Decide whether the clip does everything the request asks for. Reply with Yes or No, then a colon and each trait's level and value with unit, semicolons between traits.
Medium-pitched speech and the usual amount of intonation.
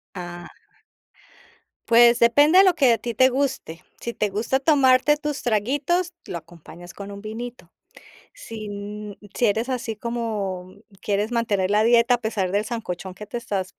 No: high, 225 Hz; average, 3.8 semitones